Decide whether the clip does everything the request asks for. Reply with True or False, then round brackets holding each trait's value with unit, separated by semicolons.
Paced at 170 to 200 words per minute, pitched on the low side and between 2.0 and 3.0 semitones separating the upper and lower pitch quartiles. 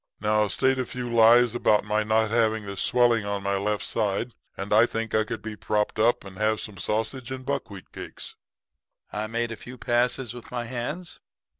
True (195 wpm; 110 Hz; 2.4 semitones)